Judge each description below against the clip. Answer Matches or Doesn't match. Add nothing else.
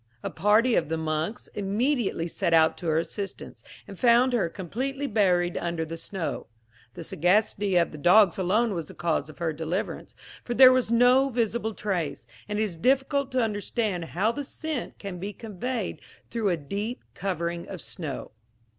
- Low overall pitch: Doesn't match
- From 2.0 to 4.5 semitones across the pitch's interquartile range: Doesn't match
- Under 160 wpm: Doesn't match